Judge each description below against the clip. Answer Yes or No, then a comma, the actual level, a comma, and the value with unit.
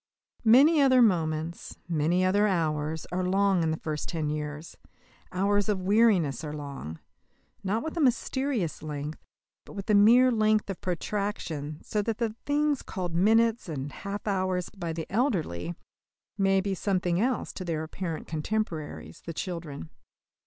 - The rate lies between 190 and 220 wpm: No, average, 150 wpm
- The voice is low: No, medium, 185 Hz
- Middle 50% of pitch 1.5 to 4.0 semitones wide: No, average, 5.3 semitones